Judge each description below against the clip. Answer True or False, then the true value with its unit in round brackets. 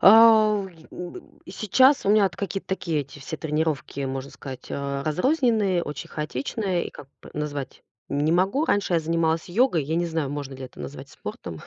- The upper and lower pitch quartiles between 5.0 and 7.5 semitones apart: True (5.5 semitones)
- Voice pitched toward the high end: False (165 Hz)